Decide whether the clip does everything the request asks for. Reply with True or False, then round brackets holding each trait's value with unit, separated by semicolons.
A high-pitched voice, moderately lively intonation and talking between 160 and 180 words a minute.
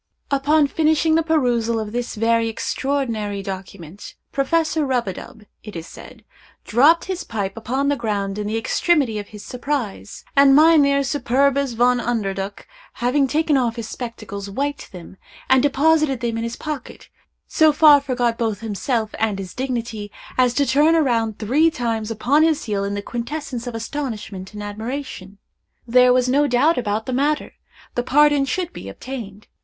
True (245 Hz; 4.7 semitones; 165 wpm)